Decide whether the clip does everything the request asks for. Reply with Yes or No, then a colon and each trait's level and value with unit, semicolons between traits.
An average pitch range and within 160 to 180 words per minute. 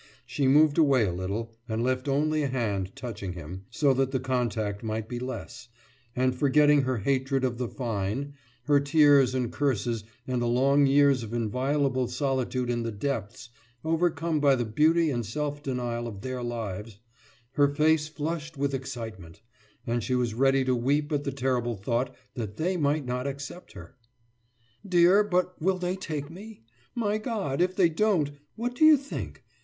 Yes: average, 4.0 semitones; average, 175 wpm